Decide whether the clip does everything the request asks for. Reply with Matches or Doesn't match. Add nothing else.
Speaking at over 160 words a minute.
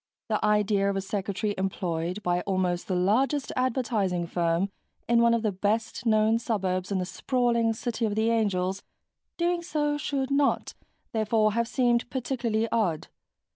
Doesn't match